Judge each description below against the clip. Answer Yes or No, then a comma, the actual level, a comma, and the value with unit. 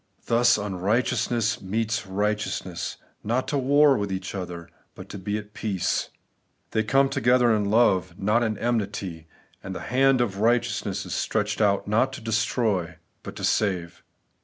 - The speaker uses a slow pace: No, average, 160 wpm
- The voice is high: No, low, 105 Hz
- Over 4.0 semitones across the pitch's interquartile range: No, average, 3.7 semitones